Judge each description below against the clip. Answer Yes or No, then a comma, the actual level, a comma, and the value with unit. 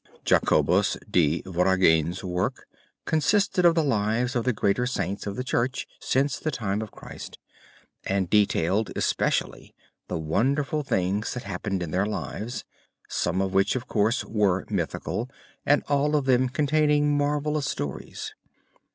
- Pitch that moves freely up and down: Yes, wide, 6.7 semitones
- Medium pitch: No, low, 110 Hz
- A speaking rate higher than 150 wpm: No, average, 145 wpm